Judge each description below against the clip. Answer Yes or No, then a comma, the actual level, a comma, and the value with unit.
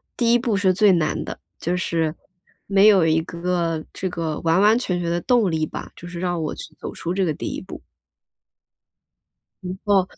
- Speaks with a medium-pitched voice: Yes, medium, 180 Hz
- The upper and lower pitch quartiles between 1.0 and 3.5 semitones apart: Yes, average, 3.0 semitones